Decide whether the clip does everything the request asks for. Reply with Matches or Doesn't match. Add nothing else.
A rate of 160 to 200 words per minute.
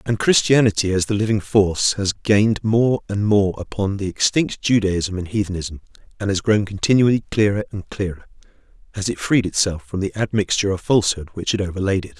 Matches